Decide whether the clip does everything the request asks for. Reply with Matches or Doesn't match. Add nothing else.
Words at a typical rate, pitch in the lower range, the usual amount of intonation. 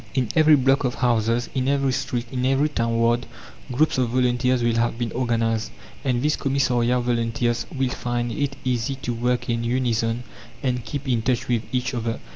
Doesn't match